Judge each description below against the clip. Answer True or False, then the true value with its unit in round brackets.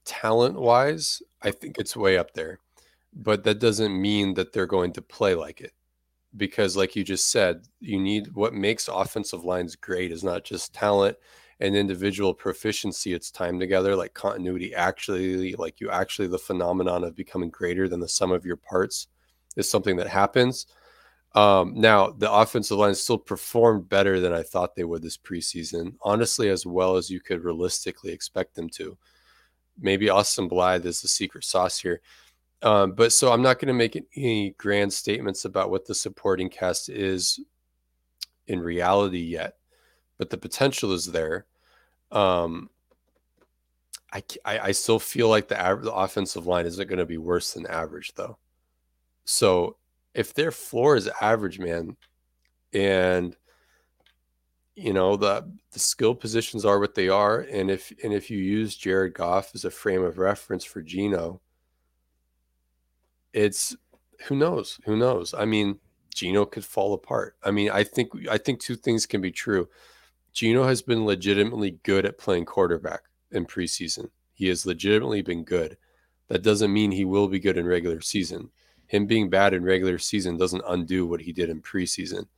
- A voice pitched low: True (95 Hz)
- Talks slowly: False (170 wpm)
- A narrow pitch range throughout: False (3.2 semitones)